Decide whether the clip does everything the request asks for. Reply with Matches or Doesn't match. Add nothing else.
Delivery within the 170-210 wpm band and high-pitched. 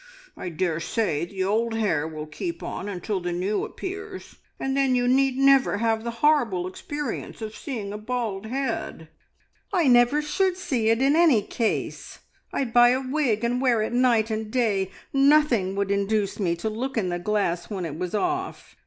Matches